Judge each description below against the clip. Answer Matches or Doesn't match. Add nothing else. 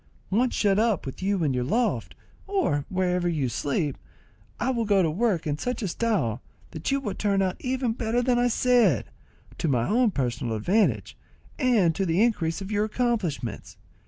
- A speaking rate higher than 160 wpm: Matches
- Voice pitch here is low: Doesn't match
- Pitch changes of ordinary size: Doesn't match